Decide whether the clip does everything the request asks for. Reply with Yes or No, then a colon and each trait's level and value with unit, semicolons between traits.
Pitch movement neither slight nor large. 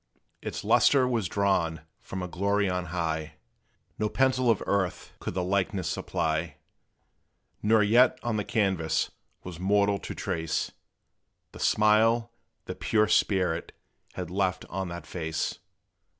Yes: average, 3.7 semitones